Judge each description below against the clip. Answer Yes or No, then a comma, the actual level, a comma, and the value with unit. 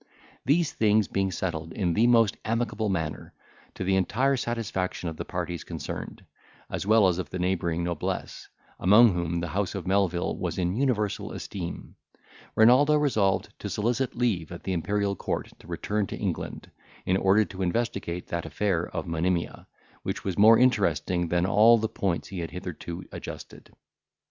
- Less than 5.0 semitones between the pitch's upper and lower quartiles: Yes, average, 4.1 semitones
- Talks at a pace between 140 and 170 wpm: Yes, average, 165 wpm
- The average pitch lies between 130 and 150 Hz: No, very low, 95 Hz